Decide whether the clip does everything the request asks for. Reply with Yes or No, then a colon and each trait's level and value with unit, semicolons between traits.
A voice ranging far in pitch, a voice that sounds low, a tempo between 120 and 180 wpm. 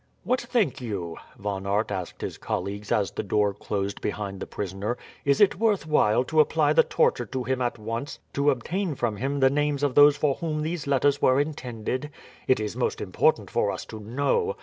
No: wide, 5.9 semitones; low, 130 Hz; average, 200 wpm